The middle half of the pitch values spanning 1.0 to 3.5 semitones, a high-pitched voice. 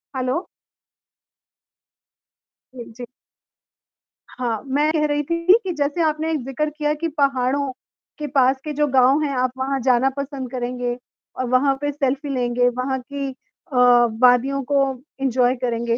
Yes: narrow, 2.6 semitones; very high, 270 Hz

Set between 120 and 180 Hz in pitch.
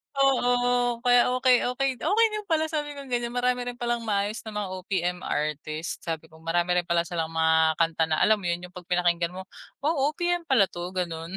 No: high, 200 Hz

